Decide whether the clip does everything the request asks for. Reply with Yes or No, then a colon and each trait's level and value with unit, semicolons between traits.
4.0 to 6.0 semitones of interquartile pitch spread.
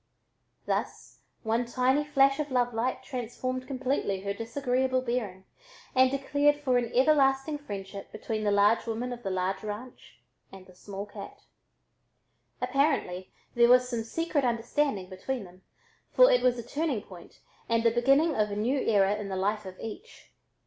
Yes: average, 4.6 semitones